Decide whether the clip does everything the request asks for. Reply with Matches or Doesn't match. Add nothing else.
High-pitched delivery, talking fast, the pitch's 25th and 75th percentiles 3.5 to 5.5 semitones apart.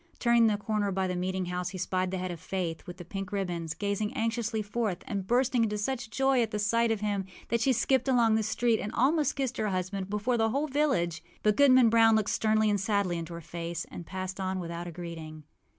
Matches